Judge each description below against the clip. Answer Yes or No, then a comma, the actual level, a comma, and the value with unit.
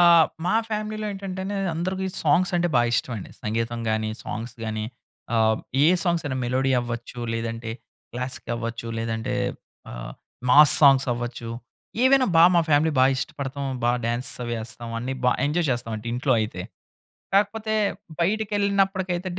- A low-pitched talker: Yes, low, 130 Hz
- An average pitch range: No, wide, 7.4 semitones